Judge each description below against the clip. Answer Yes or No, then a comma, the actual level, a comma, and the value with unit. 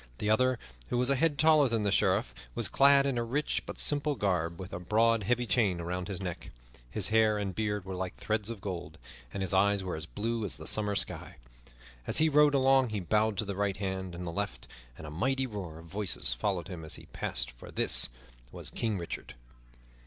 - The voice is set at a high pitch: No, low, 105 Hz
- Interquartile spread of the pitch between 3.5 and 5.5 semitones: Yes, average, 4.7 semitones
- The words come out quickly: Yes, fast, 220 wpm